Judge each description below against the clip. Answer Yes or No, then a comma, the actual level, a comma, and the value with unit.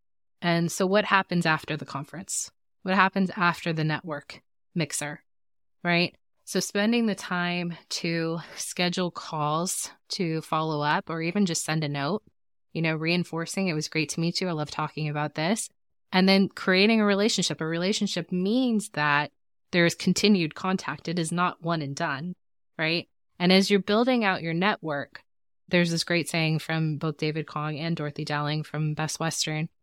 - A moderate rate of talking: Yes, average, 170 wpm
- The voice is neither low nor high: Yes, medium, 165 Hz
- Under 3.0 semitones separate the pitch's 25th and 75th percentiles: No, average, 3.4 semitones